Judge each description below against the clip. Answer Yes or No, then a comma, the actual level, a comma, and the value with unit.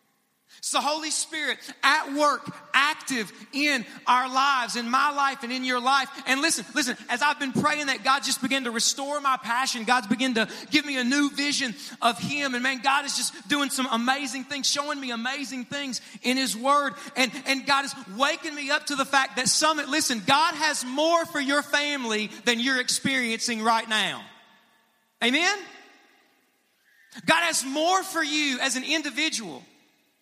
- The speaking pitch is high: Yes, very high, 270 Hz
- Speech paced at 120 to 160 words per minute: No, average, 180 wpm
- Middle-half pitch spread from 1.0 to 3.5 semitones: Yes, average, 2.7 semitones